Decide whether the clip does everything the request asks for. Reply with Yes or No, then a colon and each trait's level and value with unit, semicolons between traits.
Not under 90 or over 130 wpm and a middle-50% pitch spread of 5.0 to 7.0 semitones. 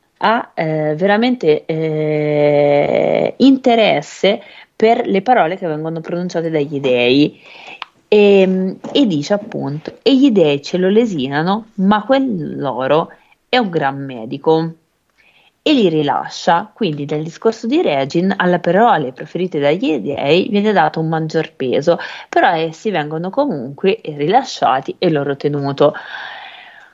Yes: average, 125 wpm; wide, 5.5 semitones